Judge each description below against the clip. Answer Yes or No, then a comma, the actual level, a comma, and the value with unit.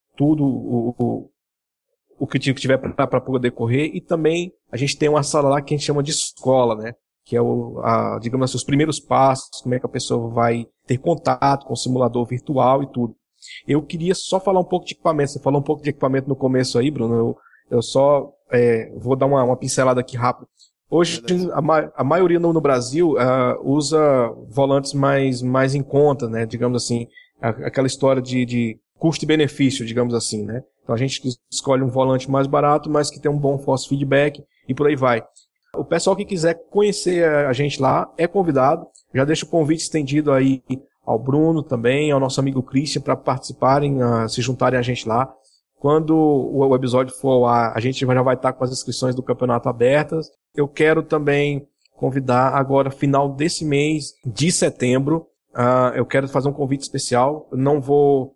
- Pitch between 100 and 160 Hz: Yes, low, 135 Hz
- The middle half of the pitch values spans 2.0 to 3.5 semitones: Yes, average, 2.8 semitones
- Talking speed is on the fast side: Yes, fast, 195 wpm